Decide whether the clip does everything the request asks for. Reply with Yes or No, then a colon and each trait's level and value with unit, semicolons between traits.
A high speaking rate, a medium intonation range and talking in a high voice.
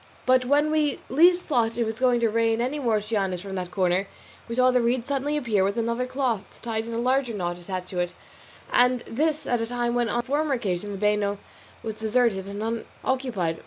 Yes: fast, 220 wpm; average, 3.8 semitones; high, 230 Hz